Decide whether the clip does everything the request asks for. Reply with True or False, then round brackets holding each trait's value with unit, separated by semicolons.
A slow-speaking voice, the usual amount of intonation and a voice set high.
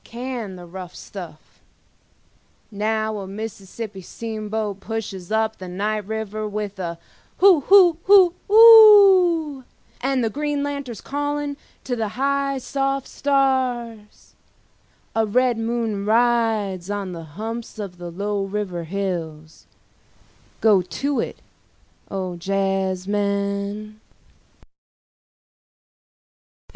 True (105 wpm; 5.0 semitones; 215 Hz)